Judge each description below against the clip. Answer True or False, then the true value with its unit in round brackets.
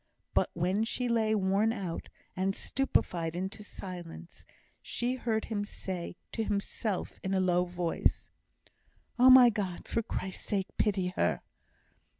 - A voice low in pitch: False (195 Hz)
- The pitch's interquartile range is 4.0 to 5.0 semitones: False (3.5 semitones)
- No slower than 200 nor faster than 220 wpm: False (140 wpm)